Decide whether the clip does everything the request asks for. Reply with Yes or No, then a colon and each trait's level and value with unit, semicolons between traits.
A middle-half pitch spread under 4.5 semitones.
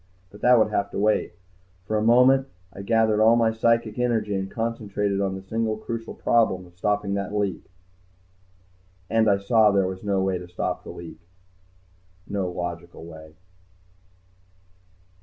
Yes: average, 2.8 semitones